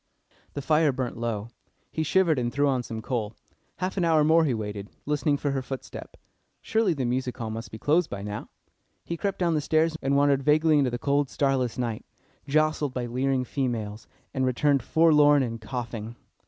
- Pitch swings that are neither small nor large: Yes, average, 4.2 semitones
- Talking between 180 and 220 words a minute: Yes, average, 190 wpm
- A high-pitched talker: No, low, 135 Hz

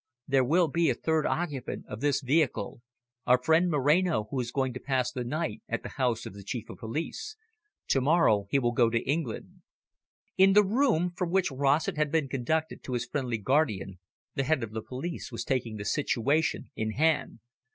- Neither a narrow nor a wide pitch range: Yes, average, 4.8 semitones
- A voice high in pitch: No, low, 135 Hz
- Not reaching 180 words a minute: No, average, 195 wpm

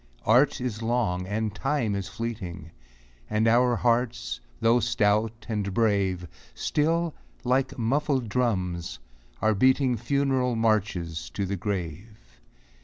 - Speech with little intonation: No, average, 4.2 semitones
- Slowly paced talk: Yes, slow, 115 wpm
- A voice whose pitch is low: Yes, low, 110 Hz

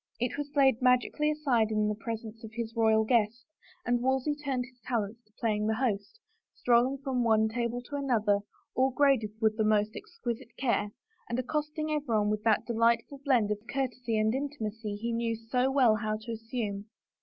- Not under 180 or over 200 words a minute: Yes, average, 190 wpm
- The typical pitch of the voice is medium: No, high, 235 Hz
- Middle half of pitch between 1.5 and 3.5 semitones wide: Yes, average, 3.2 semitones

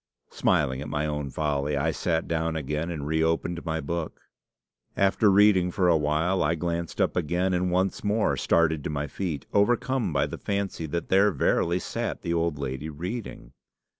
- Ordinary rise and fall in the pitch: Yes, average, 3.5 semitones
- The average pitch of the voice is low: Yes, very low, 85 Hz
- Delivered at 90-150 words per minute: No, average, 175 wpm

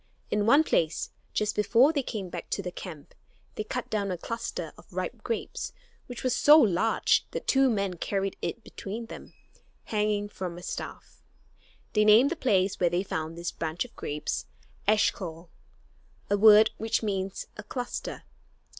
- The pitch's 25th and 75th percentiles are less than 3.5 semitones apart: No, average, 3.9 semitones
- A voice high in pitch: Yes, high, 210 Hz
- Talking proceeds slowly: No, average, 165 wpm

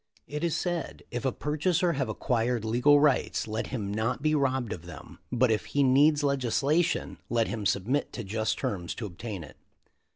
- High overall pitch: No, low, 125 Hz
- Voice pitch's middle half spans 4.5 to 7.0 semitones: Yes, average, 4.9 semitones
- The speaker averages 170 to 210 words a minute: Yes, average, 190 wpm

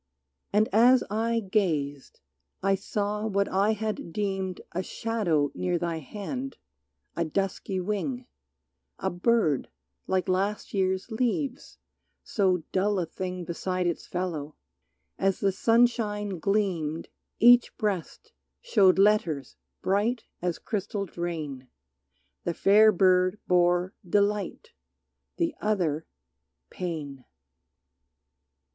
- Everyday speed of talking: No, slow, 105 wpm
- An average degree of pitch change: Yes, average, 3.4 semitones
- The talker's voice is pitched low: No, high, 195 Hz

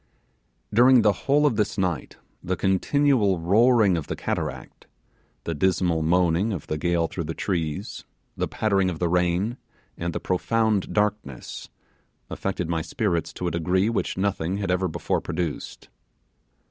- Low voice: Yes, very low, 95 Hz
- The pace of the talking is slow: No, average, 150 wpm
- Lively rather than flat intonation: No, average, 3.7 semitones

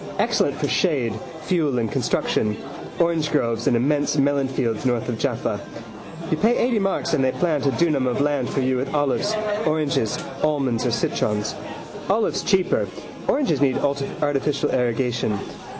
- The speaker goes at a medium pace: Yes, average, 145 wpm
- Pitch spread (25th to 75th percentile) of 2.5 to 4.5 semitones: Yes, average, 3.9 semitones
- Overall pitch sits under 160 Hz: Yes, medium, 140 Hz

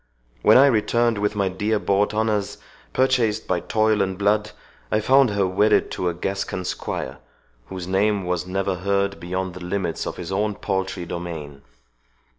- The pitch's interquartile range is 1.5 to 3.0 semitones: Yes, narrow, 2.6 semitones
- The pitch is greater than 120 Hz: No, low, 100 Hz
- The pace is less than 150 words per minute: No, average, 165 wpm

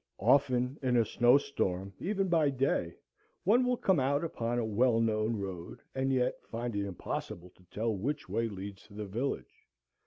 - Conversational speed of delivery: Yes, average, 180 wpm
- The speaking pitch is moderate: No, low, 120 Hz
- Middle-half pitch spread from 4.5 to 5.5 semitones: Yes, average, 5.2 semitones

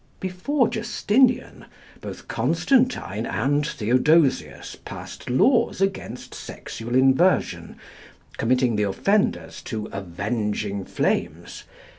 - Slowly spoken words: Yes, slow, 85 wpm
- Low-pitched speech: Yes, low, 130 Hz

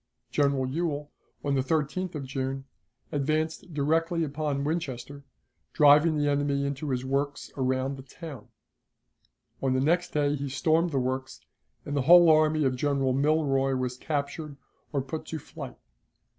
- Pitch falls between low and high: Yes, medium, 145 Hz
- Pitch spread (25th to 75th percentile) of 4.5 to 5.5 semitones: No, narrow, 2.5 semitones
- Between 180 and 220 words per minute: No, average, 150 wpm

